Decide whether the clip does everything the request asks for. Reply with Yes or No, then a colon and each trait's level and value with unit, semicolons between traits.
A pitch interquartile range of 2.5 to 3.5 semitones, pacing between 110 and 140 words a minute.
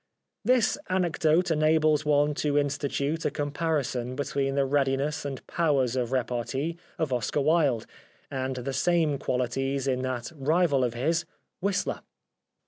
Yes: average, 3.2 semitones; slow, 135 wpm